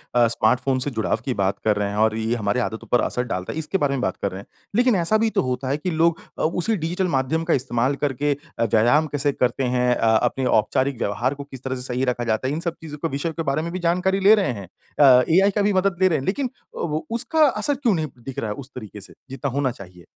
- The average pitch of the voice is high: No, low, 135 Hz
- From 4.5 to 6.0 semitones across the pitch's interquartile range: Yes, wide, 5.5 semitones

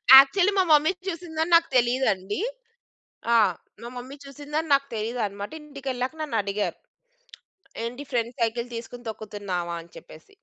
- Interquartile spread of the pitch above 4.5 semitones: Yes, wide, 5.5 semitones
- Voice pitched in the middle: No, high, 245 Hz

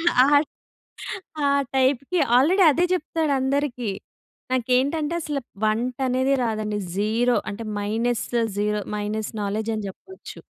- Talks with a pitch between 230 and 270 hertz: Yes, very high, 250 Hz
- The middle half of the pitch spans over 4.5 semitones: Yes, average, 4.9 semitones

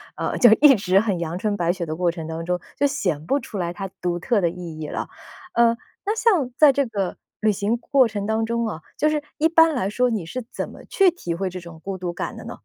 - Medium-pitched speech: No, high, 205 Hz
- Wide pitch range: Yes, wide, 6.3 semitones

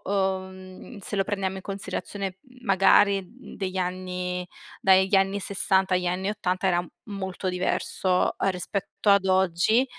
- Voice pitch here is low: No, high, 190 Hz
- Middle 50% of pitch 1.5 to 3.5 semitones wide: No, narrow, 1.1 semitones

